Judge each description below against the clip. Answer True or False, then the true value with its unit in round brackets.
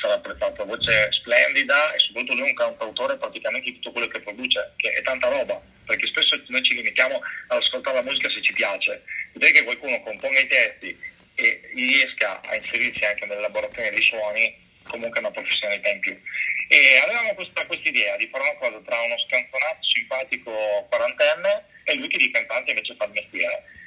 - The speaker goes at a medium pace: False (185 wpm)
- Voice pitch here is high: True (295 Hz)